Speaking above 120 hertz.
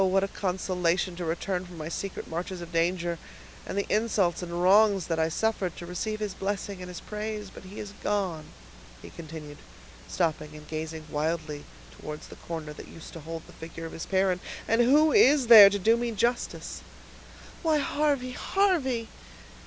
Yes: medium, 185 Hz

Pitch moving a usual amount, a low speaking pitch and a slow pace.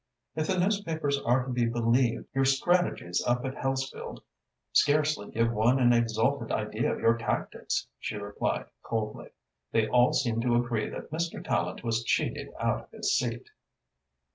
No: average, 3.3 semitones; low, 120 Hz; average, 160 wpm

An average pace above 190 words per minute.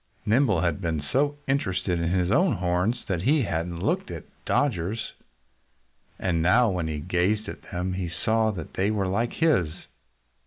No: average, 165 wpm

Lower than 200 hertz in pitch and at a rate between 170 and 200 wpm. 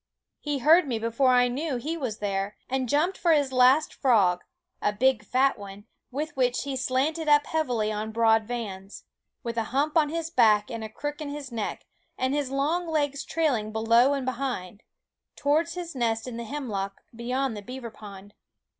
No: very high, 255 Hz; average, 190 wpm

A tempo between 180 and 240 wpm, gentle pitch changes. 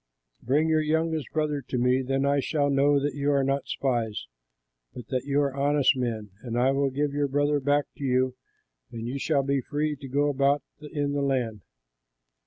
Yes: average, 195 wpm; narrow, 1.9 semitones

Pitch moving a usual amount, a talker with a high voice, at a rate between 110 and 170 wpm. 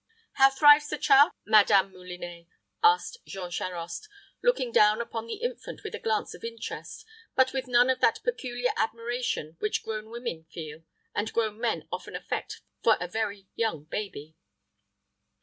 No: wide, 6.3 semitones; high, 225 Hz; average, 155 wpm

